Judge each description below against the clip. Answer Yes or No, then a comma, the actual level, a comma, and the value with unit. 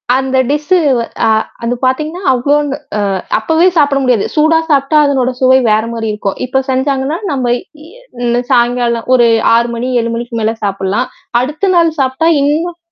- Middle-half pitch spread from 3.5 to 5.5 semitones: Yes, average, 3.8 semitones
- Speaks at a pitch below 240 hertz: No, very high, 260 Hz